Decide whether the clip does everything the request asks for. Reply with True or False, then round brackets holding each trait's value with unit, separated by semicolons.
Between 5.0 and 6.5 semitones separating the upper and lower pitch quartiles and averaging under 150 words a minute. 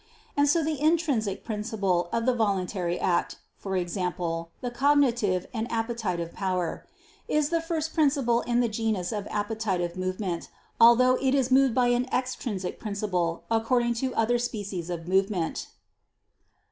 True (5.3 semitones; 140 wpm)